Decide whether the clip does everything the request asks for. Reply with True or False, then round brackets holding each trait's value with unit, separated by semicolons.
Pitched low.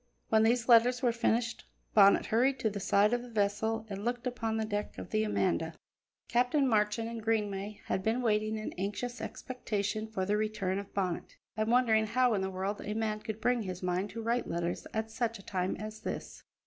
False (220 Hz)